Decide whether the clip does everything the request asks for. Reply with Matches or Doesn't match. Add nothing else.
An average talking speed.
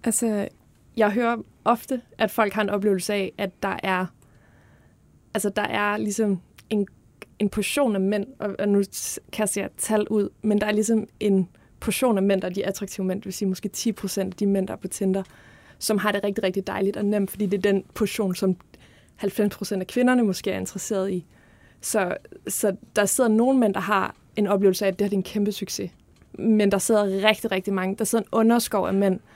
Matches